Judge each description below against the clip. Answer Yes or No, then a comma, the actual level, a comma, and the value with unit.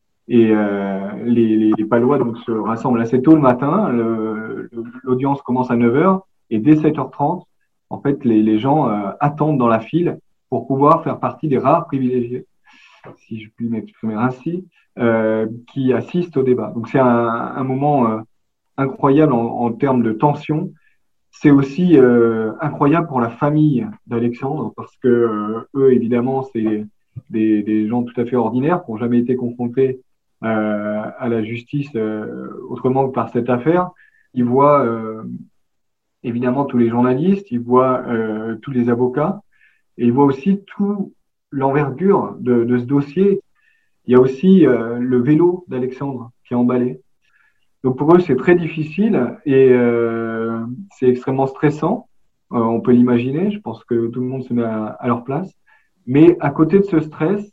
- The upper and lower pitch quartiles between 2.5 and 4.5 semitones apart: Yes, average, 3.9 semitones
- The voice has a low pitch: Yes, low, 125 Hz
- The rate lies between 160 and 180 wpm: Yes, average, 170 wpm